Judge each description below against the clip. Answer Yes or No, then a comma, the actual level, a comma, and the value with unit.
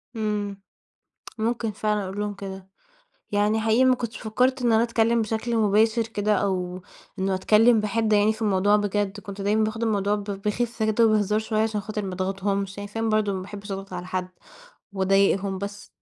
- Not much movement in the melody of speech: Yes, narrow, 2.0 semitones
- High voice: Yes, high, 210 Hz